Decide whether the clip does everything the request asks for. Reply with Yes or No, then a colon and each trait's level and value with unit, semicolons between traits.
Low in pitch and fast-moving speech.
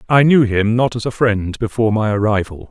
Yes: low, 110 Hz; fast, 220 wpm